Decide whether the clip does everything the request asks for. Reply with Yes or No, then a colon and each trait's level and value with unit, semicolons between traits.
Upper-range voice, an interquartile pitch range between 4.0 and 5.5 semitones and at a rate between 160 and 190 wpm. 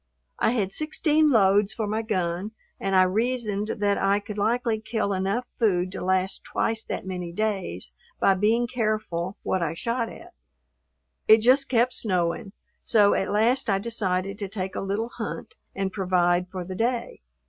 No: high, 205 Hz; average, 3.3 semitones; average, 170 wpm